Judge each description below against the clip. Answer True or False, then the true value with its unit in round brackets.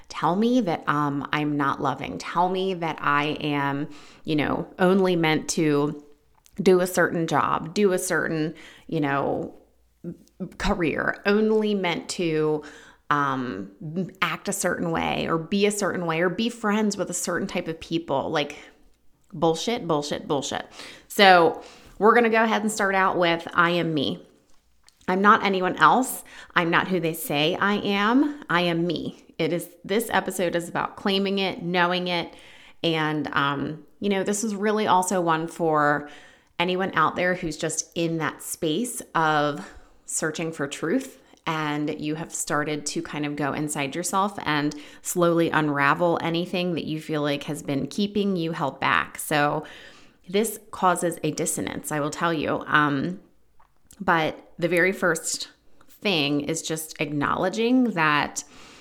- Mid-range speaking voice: True (170 Hz)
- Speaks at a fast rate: False (155 wpm)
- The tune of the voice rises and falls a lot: False (3.9 semitones)